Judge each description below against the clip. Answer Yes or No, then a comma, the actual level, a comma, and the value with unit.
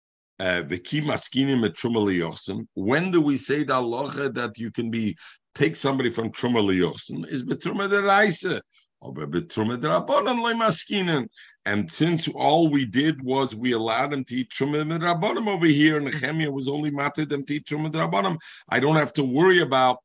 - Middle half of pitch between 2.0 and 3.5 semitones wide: No, average, 4.5 semitones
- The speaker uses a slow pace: Yes, slow, 130 wpm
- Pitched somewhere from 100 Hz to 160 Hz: Yes, medium, 140 Hz